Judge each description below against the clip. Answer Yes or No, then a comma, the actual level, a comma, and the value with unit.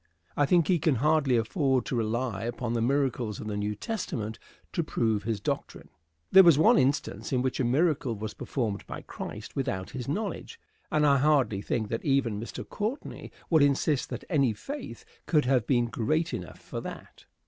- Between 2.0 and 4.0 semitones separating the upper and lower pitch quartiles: No, average, 5.1 semitones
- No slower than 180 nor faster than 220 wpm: Yes, average, 185 wpm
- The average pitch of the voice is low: Yes, low, 130 Hz